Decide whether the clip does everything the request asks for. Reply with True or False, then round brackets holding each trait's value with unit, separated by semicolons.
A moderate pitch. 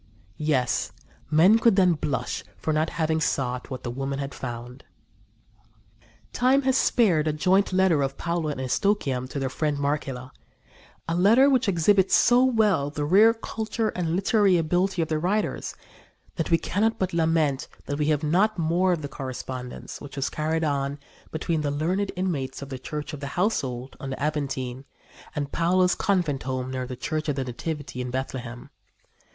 True (155 Hz)